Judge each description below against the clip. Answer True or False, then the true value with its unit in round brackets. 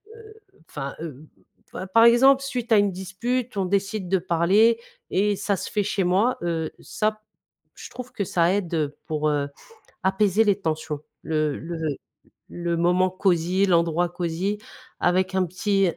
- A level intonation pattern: False (3.6 semitones)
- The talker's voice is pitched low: False (185 Hz)